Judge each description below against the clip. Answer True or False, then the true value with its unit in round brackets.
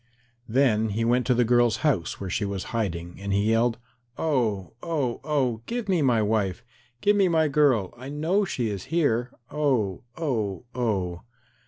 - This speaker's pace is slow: False (170 wpm)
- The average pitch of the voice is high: False (120 Hz)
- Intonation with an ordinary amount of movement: False (6.2 semitones)